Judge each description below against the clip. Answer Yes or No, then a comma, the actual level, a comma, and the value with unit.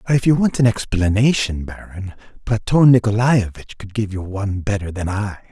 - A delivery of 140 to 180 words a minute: Yes, average, 165 wpm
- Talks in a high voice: No, low, 105 Hz